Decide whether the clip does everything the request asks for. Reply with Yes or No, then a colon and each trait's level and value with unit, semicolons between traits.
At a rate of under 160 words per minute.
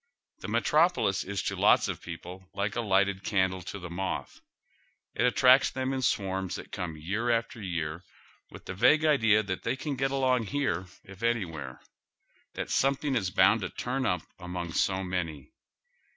No: average, 175 wpm